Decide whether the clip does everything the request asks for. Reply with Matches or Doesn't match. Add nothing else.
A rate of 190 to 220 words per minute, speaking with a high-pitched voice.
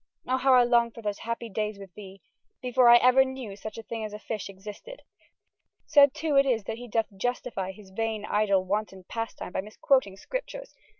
Matches